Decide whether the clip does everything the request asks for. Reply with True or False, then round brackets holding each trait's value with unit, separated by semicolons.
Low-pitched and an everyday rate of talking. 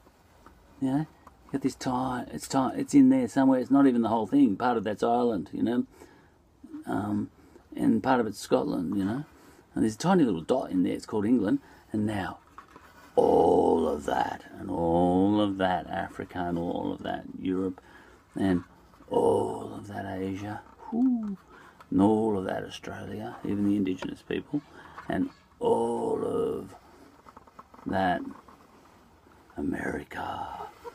True (130 Hz; 150 wpm)